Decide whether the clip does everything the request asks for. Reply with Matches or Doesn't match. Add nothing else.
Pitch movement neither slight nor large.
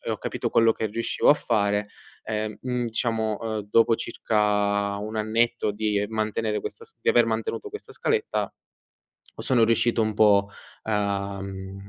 Doesn't match